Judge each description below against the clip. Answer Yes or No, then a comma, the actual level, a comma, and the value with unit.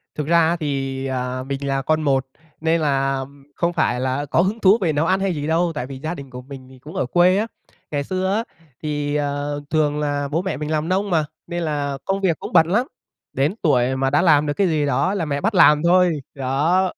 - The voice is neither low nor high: Yes, medium, 150 Hz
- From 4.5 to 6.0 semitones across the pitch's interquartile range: No, average, 3.9 semitones